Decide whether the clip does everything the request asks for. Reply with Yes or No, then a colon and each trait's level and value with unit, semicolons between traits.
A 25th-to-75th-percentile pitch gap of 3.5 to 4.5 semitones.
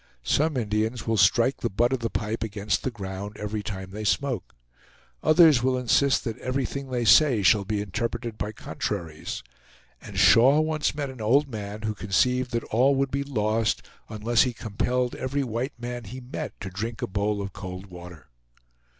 Yes: average, 3.8 semitones